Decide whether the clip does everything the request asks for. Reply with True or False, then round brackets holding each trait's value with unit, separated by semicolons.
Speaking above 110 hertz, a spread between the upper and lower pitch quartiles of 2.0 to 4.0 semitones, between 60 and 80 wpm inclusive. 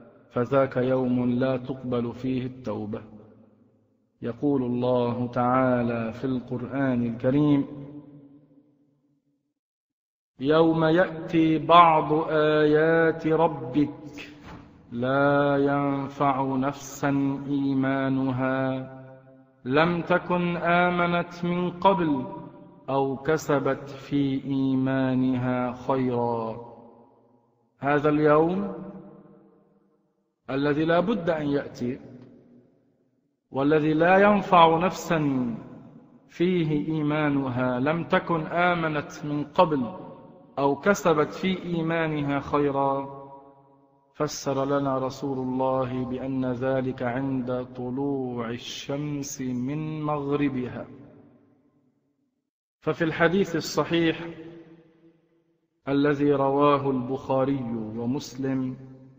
True (140 Hz; 3.3 semitones; 75 wpm)